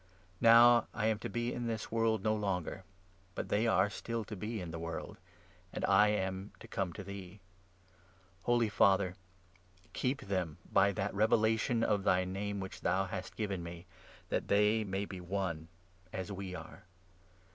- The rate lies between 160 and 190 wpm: Yes, average, 170 wpm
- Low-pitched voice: Yes, low, 100 Hz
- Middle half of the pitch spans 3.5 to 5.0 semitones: No, average, 2.7 semitones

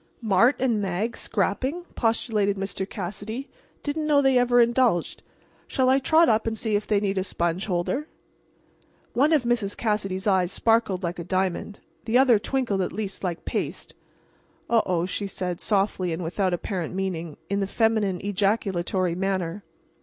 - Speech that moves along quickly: No, average, 160 wpm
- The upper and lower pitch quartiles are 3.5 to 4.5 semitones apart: Yes, average, 4.0 semitones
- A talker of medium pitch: No, high, 200 Hz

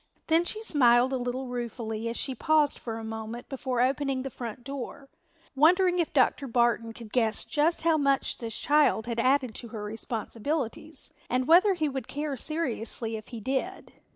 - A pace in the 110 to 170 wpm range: No, average, 180 wpm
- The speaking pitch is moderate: No, very high, 255 Hz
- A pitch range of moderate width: Yes, average, 4.3 semitones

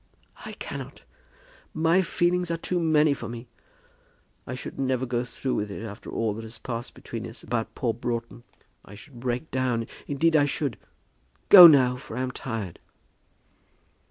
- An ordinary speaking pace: Yes, average, 165 wpm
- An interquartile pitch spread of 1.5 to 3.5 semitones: No, average, 4.5 semitones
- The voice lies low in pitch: Yes, low, 125 Hz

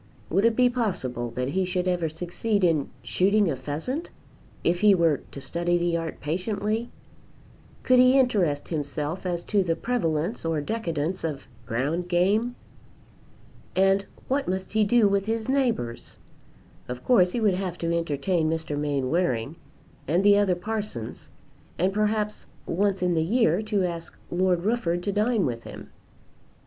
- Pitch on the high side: No, medium, 180 Hz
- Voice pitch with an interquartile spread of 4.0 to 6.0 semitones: Yes, average, 4.7 semitones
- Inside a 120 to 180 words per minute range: Yes, average, 155 wpm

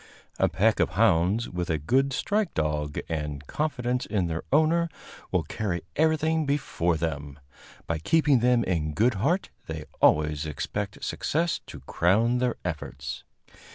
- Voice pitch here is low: Yes, low, 100 Hz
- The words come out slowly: No, average, 145 wpm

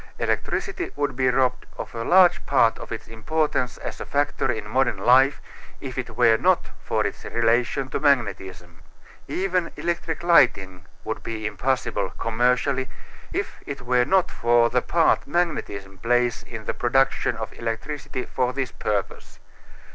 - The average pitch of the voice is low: Yes, low, 125 Hz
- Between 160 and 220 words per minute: No, average, 150 wpm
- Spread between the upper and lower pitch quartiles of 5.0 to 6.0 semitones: No, average, 4.0 semitones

